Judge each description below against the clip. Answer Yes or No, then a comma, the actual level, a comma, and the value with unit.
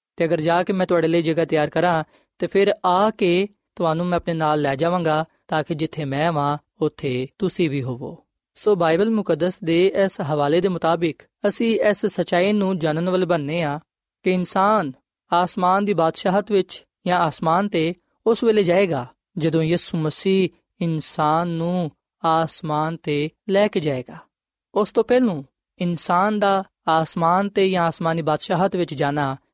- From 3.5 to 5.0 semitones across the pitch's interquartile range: No, average, 3.1 semitones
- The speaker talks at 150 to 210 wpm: Yes, fast, 165 wpm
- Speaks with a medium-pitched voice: Yes, medium, 170 Hz